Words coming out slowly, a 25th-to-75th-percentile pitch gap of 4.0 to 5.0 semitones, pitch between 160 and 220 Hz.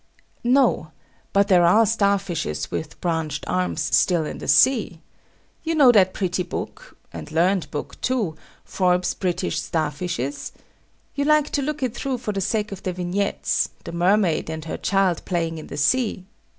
No: average, 170 wpm; average, 4.5 semitones; medium, 185 Hz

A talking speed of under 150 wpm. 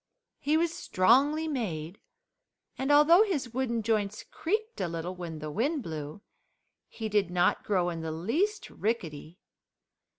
Yes: average, 140 wpm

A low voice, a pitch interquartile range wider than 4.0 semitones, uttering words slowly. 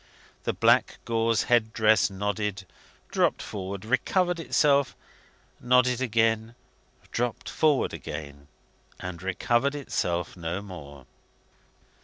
Yes: low, 110 Hz; average, 5.0 semitones; slow, 100 wpm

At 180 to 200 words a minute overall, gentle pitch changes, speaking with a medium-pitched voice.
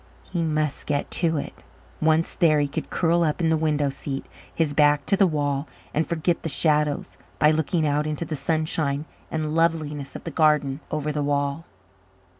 Yes: average, 185 wpm; narrow, 1.9 semitones; medium, 155 Hz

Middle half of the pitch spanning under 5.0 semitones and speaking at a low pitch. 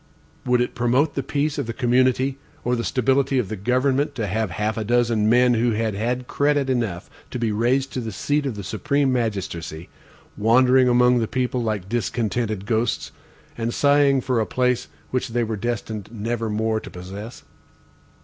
Yes: average, 2.7 semitones; low, 120 Hz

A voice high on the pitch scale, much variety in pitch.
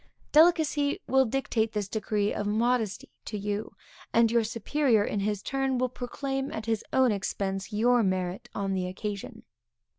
No: high, 220 Hz; average, 4.0 semitones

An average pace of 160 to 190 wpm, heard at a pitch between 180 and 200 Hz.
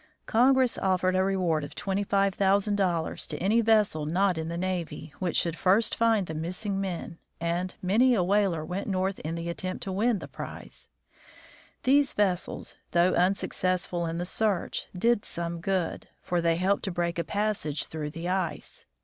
Yes: average, 165 wpm; medium, 185 Hz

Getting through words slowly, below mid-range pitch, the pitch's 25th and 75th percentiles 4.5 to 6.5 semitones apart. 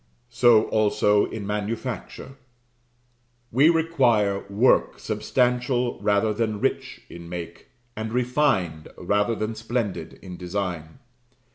No: slow, 105 wpm; low, 110 Hz; average, 3.6 semitones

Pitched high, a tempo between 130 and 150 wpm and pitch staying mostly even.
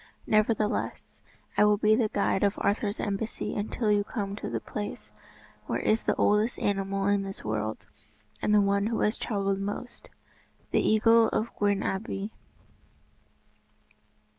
Yes: high, 205 Hz; average, 145 wpm; narrow, 1.5 semitones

